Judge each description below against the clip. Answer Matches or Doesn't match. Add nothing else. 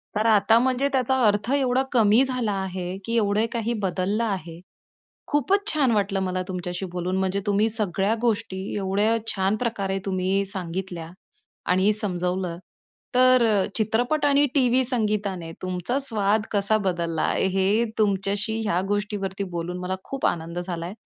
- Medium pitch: Doesn't match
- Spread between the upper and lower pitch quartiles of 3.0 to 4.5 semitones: Matches